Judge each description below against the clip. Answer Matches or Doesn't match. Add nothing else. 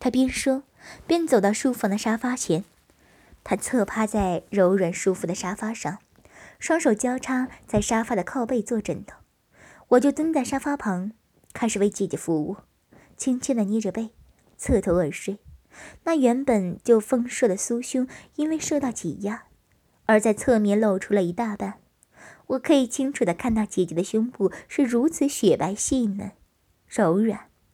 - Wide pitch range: Doesn't match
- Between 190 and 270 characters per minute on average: Matches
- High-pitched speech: Matches